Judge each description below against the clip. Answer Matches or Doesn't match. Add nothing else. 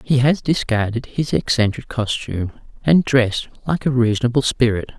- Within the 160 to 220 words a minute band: Doesn't match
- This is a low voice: Matches